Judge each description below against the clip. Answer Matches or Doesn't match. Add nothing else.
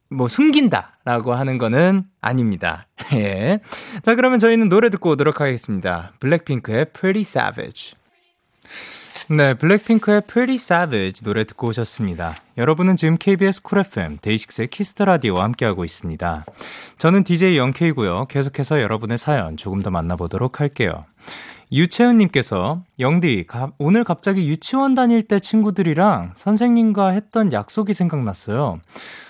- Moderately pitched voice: Matches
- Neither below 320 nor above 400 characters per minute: Matches